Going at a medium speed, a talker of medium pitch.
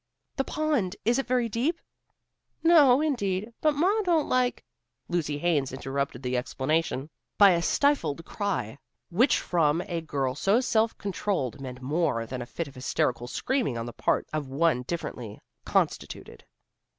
Yes: average, 155 wpm; medium, 170 Hz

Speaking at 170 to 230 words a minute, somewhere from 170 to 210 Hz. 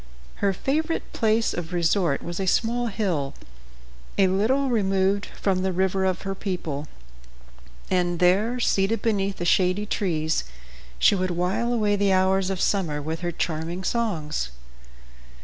No: average, 145 wpm; high, 190 Hz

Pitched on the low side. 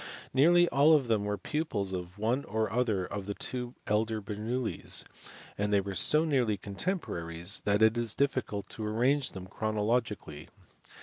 Yes: low, 110 Hz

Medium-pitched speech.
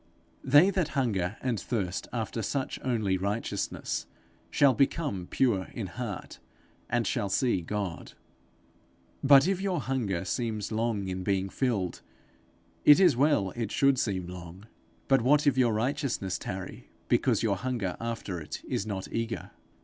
No: low, 115 Hz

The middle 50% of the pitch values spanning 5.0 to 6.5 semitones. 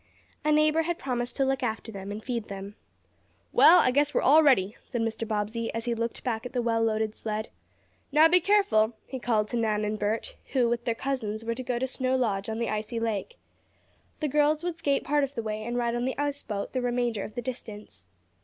No: average, 3.7 semitones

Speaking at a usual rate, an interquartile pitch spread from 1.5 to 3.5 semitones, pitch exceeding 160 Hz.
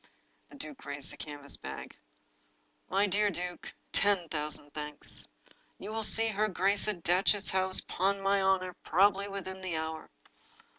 Yes: average, 150 wpm; average, 3.1 semitones; high, 190 Hz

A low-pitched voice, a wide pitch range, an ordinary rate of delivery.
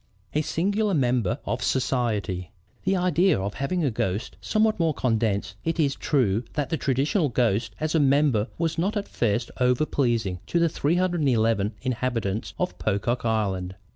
Yes: low, 130 Hz; wide, 6.9 semitones; average, 155 wpm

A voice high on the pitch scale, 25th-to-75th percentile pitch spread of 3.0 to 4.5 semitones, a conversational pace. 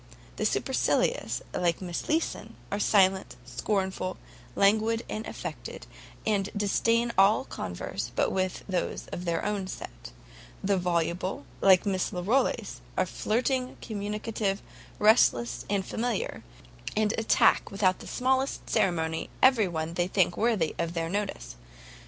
No: high, 195 Hz; average, 3.6 semitones; slow, 125 wpm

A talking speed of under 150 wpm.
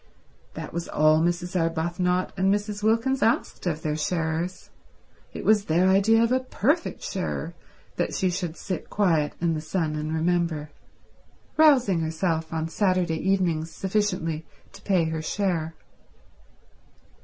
Yes: average, 140 wpm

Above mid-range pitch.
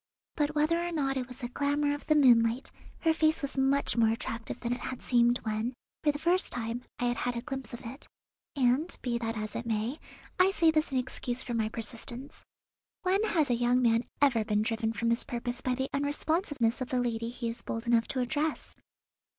Yes: very high, 250 Hz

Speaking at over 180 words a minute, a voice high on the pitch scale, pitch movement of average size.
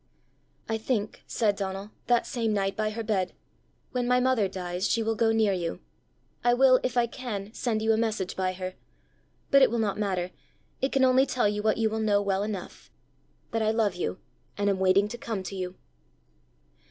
Yes: average, 200 wpm; high, 215 Hz; average, 3.1 semitones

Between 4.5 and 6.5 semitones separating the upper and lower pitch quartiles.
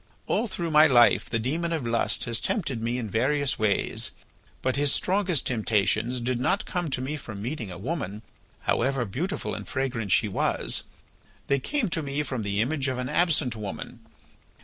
Yes: average, 5.1 semitones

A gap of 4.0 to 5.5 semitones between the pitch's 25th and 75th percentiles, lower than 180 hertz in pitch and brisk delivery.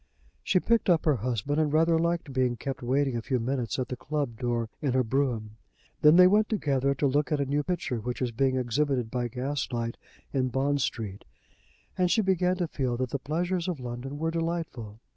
Yes: average, 4.7 semitones; low, 135 Hz; fast, 210 wpm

